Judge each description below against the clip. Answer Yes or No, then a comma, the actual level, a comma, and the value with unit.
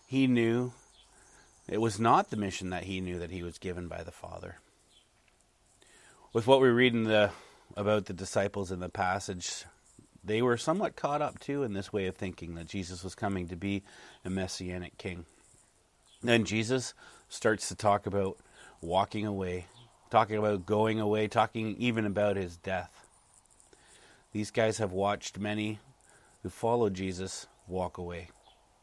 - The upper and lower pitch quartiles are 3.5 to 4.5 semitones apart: No, average, 3.1 semitones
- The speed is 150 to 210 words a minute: Yes, average, 160 wpm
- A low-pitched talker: Yes, low, 100 Hz